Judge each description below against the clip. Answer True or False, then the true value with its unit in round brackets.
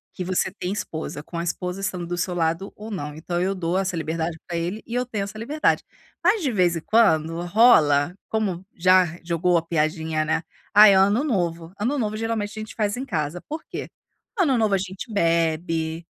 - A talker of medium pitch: True (180 Hz)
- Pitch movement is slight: False (4.2 semitones)